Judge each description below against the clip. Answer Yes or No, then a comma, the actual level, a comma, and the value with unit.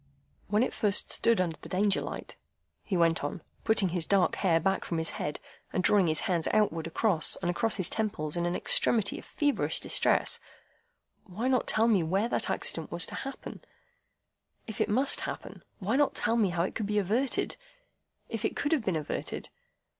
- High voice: Yes, high, 200 Hz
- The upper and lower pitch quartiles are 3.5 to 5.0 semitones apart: Yes, average, 4.7 semitones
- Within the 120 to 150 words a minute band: No, average, 185 wpm